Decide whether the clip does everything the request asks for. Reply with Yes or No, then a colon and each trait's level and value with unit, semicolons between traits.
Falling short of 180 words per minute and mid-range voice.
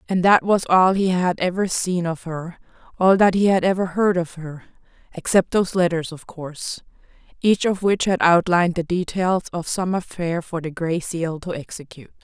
No: average, 185 wpm; medium, 175 Hz